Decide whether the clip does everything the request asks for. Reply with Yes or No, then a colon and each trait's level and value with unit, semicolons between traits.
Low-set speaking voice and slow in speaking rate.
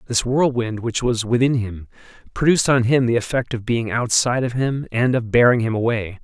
No: low, 120 Hz; average, 200 wpm